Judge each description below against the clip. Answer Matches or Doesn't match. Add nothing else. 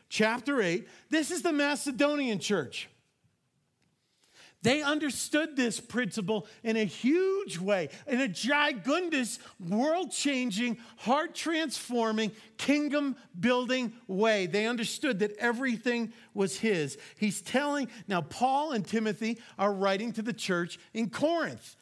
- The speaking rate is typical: Doesn't match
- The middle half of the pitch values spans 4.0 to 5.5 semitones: Matches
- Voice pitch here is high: Matches